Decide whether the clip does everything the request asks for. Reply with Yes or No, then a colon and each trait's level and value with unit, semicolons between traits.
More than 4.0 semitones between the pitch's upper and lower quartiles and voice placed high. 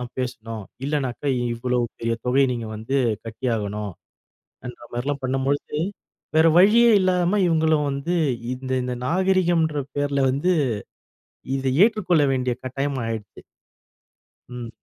No: average, 4.5 semitones; low, 135 Hz